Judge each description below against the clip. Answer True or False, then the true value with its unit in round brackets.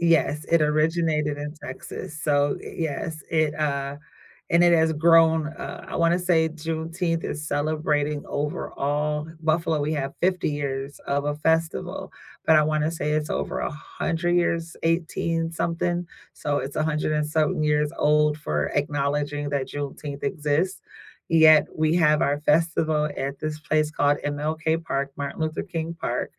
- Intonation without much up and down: True (1.8 semitones)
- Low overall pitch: False (155 Hz)